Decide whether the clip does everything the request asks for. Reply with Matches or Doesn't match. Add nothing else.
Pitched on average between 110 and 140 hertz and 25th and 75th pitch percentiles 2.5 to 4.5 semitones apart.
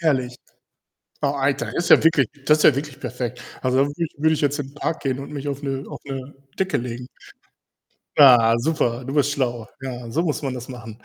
Matches